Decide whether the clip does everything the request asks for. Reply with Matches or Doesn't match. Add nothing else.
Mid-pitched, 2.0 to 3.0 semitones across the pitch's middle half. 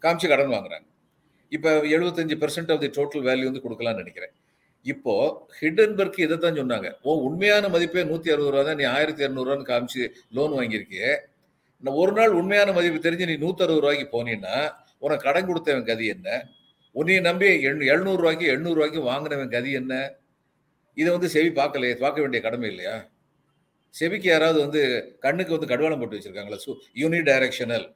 Doesn't match